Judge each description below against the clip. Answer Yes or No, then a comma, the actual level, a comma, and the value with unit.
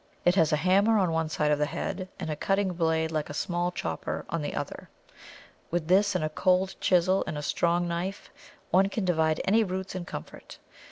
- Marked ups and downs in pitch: No, average, 2.9 semitones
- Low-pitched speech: No, medium, 175 Hz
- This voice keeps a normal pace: No, fast, 210 wpm